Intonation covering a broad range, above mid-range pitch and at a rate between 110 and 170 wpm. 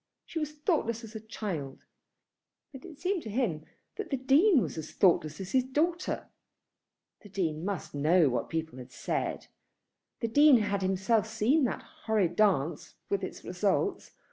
Yes: wide, 8.0 semitones; high, 220 Hz; average, 165 wpm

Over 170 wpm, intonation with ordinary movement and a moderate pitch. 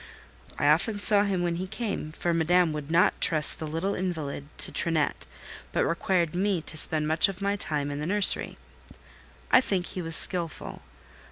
Yes: average, 180 wpm; average, 3.5 semitones; medium, 170 Hz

